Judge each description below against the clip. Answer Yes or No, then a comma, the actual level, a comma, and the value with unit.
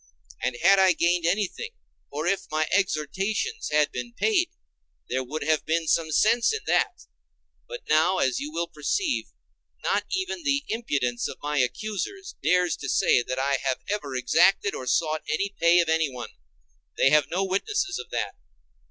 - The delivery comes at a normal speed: Yes, average, 165 wpm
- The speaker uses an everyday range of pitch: No, wide, 5.9 semitones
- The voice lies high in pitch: No, medium, 165 Hz